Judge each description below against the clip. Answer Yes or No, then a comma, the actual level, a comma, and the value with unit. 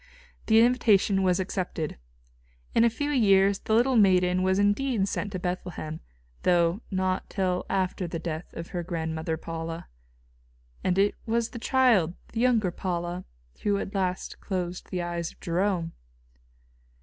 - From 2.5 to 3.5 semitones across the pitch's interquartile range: Yes, average, 3.0 semitones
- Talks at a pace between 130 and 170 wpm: Yes, average, 150 wpm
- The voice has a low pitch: No, medium, 185 Hz